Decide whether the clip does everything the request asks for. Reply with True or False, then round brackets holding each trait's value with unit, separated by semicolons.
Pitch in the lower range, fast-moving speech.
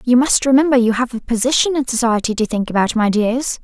False (240 Hz; 230 wpm)